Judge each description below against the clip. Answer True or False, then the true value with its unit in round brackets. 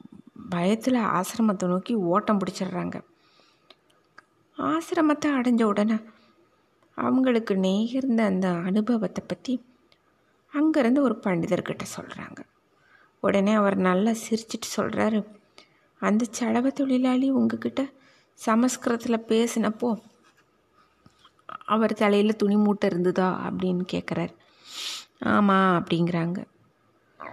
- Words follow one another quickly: False (85 wpm)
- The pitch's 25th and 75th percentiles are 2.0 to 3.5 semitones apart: False (4.0 semitones)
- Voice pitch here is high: True (220 Hz)